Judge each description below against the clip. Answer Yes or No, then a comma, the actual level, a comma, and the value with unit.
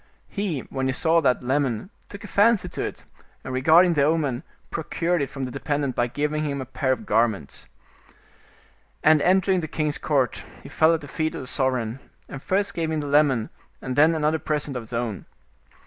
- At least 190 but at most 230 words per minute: Yes, average, 200 wpm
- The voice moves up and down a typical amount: Yes, average, 3.7 semitones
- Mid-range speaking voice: Yes, medium, 145 Hz